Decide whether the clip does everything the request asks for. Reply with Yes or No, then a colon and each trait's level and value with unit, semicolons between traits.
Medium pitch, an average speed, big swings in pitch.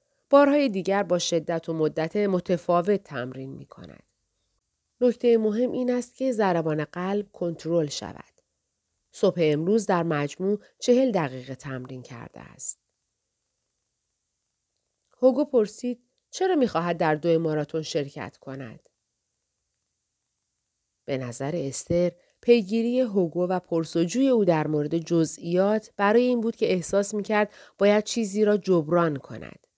Yes: medium, 180 Hz; average, 120 wpm; wide, 6.0 semitones